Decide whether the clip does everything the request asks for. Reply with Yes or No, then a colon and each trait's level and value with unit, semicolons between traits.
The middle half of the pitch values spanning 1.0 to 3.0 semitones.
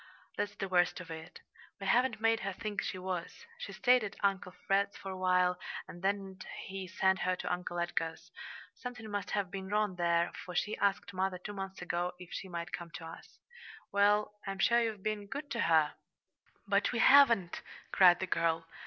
Yes: narrow, 2.5 semitones